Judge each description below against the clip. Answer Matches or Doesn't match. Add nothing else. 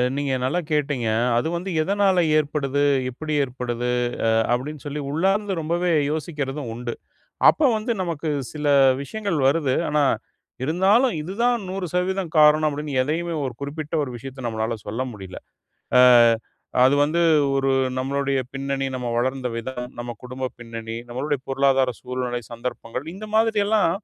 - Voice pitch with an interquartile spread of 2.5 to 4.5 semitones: Doesn't match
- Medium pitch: Matches